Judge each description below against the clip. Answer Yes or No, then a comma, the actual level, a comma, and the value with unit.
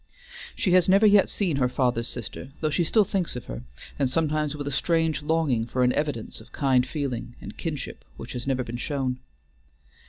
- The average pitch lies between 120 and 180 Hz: Yes, medium, 140 Hz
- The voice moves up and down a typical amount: Yes, average, 4.5 semitones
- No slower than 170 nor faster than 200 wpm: Yes, average, 195 wpm